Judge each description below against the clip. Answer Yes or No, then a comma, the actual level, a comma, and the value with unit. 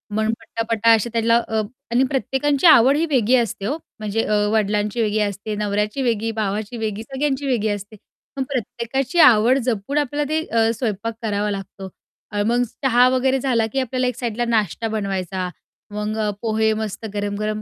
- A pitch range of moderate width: Yes, average, 3.3 semitones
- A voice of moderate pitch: No, high, 225 Hz